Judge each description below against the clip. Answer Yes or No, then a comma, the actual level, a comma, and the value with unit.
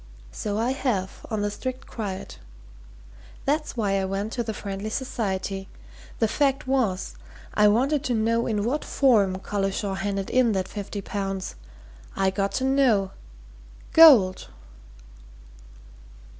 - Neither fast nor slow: No, slow, 130 wpm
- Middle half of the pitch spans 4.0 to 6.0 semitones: Yes, average, 4.5 semitones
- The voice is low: No, high, 210 Hz